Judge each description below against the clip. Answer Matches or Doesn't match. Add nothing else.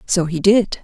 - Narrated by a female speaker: Matches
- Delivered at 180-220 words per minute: Matches